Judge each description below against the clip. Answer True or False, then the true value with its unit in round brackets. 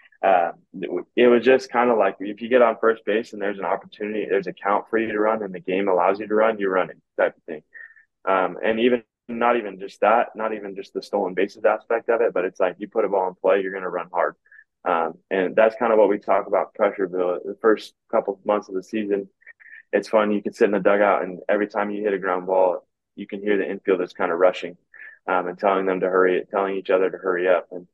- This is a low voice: True (105 Hz)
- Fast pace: True (260 wpm)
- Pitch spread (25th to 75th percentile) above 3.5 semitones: False (3.0 semitones)